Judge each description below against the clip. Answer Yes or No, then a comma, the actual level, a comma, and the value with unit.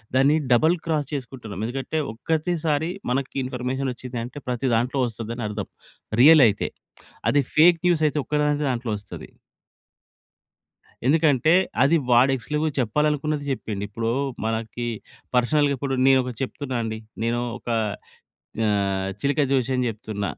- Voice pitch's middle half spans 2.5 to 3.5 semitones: No, average, 4.2 semitones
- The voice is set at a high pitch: No, low, 130 Hz